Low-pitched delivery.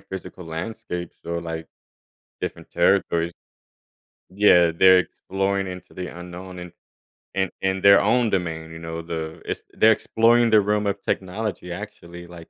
Yes: very low, 90 Hz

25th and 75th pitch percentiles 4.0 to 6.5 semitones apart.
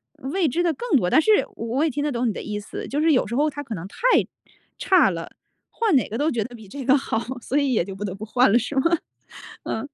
Yes: average, 5.3 semitones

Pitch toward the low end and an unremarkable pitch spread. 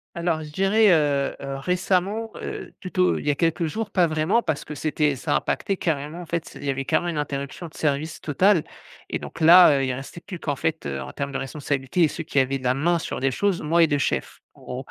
No: medium, 155 Hz; average, 3.9 semitones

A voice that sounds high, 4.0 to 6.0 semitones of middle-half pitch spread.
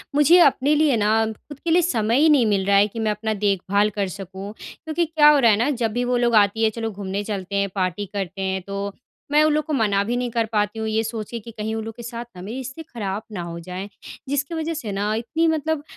Yes: high, 220 Hz; average, 5.1 semitones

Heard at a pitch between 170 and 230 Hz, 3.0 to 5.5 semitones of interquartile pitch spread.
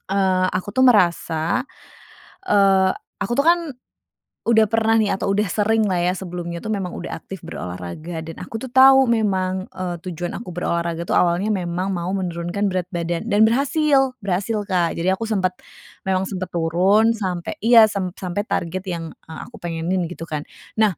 Yes: high, 190 Hz; average, 3.8 semitones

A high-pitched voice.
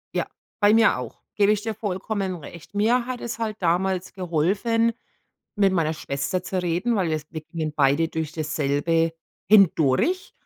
No: medium, 180 Hz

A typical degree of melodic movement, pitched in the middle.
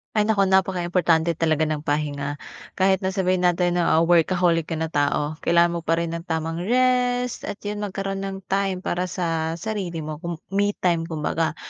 Yes: average, 3.0 semitones; medium, 175 Hz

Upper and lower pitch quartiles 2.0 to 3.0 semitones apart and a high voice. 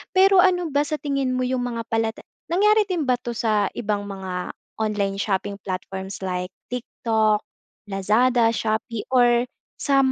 No: average, 5.0 semitones; high, 230 Hz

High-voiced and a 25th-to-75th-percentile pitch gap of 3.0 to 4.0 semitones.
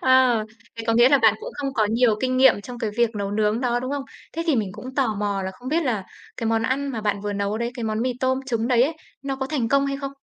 Yes: high, 240 Hz; average, 3.4 semitones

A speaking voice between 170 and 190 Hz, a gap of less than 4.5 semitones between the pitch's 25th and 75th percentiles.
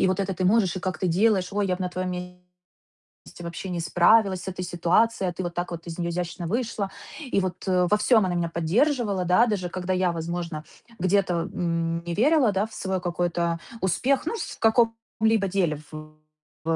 Yes: medium, 185 Hz; average, 2.8 semitones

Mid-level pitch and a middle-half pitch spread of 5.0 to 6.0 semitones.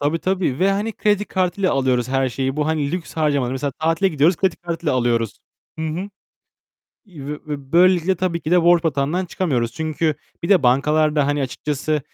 No: medium, 155 Hz; average, 4.2 semitones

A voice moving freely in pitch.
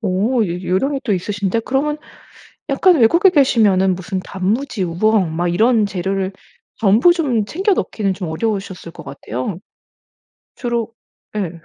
No: average, 4.9 semitones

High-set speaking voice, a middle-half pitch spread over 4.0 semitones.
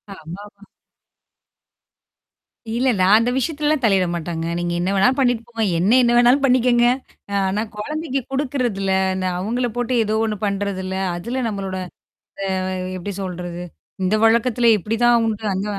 Yes: high, 220 Hz; average, 4.4 semitones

